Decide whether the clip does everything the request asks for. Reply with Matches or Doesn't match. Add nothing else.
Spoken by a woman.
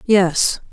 Matches